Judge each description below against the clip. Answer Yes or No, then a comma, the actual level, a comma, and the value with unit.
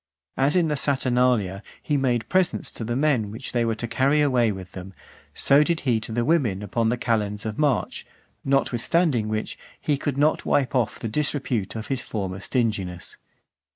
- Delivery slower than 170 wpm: No, average, 185 wpm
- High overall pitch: No, low, 120 Hz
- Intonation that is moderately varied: Yes, average, 4.6 semitones